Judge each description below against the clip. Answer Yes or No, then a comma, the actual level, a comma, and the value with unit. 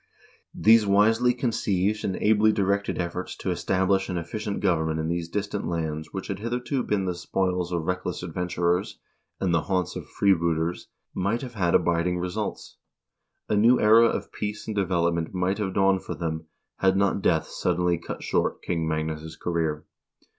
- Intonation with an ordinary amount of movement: Yes, average, 3.2 semitones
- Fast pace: No, average, 165 wpm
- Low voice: Yes, very low, 90 Hz